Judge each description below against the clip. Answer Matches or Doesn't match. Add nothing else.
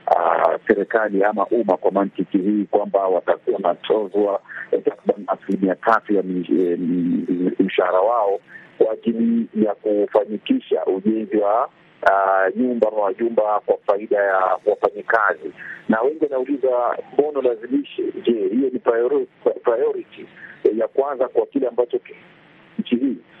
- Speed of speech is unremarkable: Doesn't match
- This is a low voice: Matches